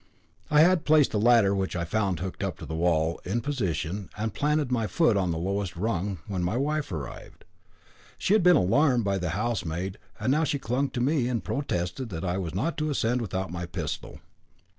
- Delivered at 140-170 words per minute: No, fast, 205 wpm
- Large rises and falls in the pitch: Yes, wide, 7.3 semitones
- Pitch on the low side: Yes, low, 105 Hz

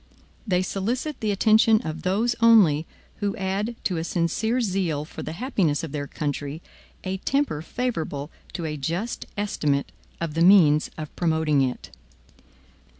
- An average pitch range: No, wide, 5.8 semitones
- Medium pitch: Yes, medium, 180 Hz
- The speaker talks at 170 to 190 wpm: No, average, 150 wpm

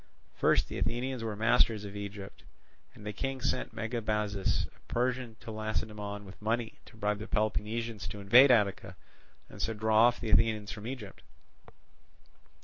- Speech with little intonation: Yes, narrow, 2.2 semitones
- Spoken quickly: No, average, 155 wpm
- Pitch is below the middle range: Yes, low, 110 Hz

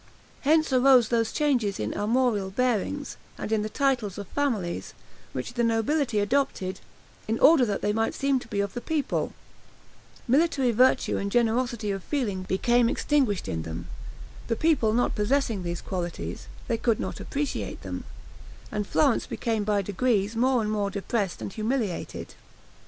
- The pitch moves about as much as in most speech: Yes, average, 4.2 semitones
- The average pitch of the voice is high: Yes, high, 225 Hz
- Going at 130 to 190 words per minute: Yes, average, 155 wpm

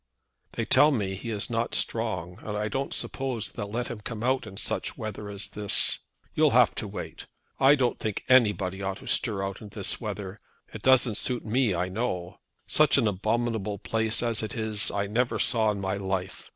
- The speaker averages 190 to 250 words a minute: Yes, average, 200 wpm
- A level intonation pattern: No, average, 3.2 semitones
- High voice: No, low, 110 Hz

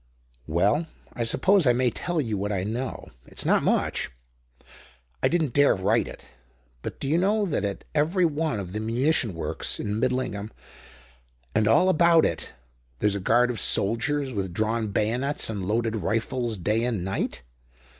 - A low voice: Yes, low, 115 Hz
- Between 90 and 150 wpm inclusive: No, average, 165 wpm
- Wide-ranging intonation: Yes, wide, 6.0 semitones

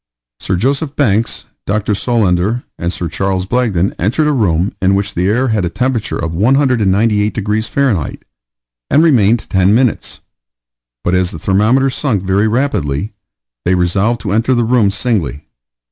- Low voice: Yes, low, 105 Hz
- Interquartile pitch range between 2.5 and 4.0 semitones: No, average, 4.5 semitones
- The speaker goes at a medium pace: Yes, average, 155 wpm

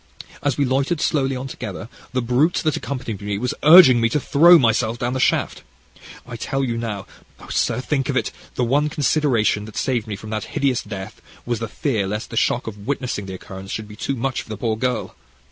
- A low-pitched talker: Yes, low, 120 Hz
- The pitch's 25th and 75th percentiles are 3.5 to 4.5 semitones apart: Yes, average, 3.9 semitones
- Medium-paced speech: No, fast, 220 wpm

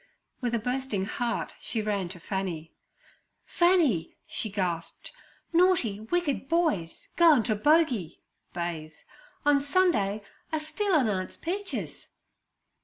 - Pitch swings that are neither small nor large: No, wide, 8.8 semitones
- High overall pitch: Yes, high, 235 Hz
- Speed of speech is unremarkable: No, slow, 110 wpm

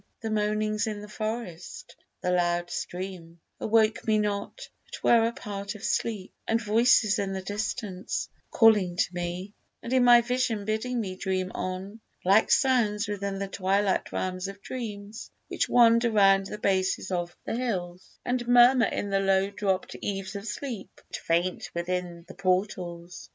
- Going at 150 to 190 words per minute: Yes, average, 160 wpm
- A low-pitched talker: No, high, 200 Hz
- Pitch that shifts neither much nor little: Yes, average, 3.1 semitones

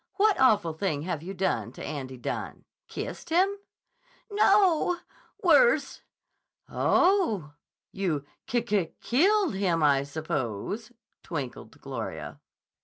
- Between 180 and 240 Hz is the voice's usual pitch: Yes, high, 190 Hz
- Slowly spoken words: Yes, slow, 110 wpm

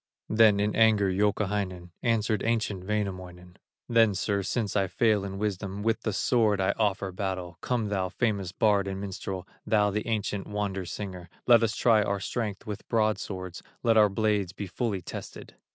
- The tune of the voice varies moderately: No, narrow, 2.3 semitones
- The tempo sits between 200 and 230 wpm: No, average, 170 wpm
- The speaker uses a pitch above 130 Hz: No, low, 100 Hz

